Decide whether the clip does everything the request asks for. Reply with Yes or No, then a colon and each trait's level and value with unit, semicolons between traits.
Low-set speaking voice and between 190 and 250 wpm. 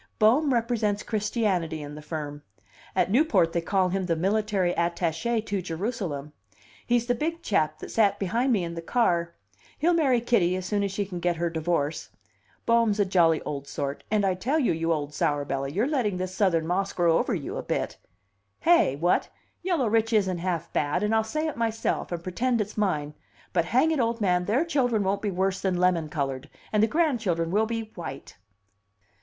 No: high, 195 Hz; average, 195 wpm